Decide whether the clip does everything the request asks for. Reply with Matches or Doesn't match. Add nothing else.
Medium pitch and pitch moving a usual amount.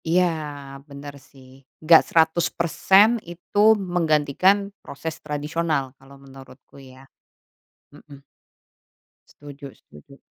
Matches